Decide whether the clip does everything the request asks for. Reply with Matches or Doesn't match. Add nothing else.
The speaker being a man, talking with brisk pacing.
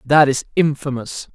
Doesn't match